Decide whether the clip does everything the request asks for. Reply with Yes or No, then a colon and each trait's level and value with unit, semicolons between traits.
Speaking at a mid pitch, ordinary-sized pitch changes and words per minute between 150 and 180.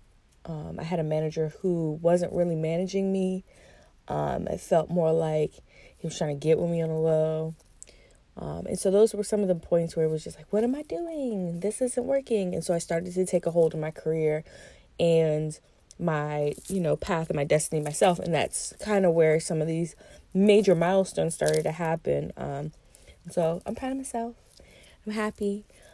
No: medium, 170 Hz; average, 3.5 semitones; average, 200 wpm